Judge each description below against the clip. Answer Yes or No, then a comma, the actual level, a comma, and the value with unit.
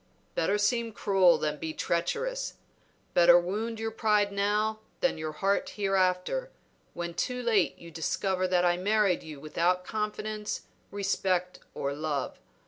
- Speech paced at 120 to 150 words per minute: Yes, slow, 135 wpm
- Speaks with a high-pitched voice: Yes, high, 195 Hz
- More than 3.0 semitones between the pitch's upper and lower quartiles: Yes, average, 3.8 semitones